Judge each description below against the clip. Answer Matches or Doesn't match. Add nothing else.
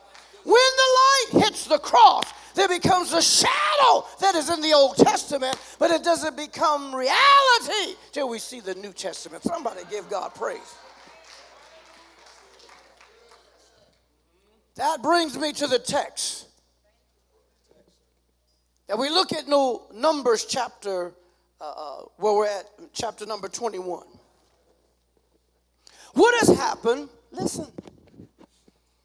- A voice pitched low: Doesn't match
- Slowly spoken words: Matches